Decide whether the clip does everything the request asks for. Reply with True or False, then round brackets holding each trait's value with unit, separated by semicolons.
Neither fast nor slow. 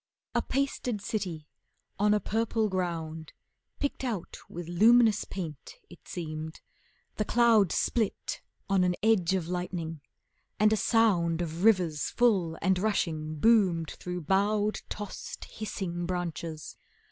False (125 wpm)